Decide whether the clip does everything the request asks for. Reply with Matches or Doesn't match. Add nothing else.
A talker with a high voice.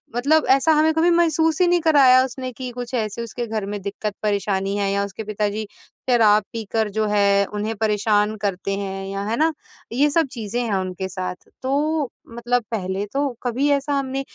Matches